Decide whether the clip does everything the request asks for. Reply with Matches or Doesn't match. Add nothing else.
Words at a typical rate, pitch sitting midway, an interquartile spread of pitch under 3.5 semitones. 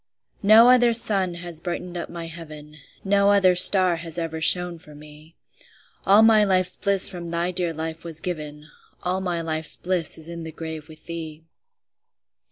Matches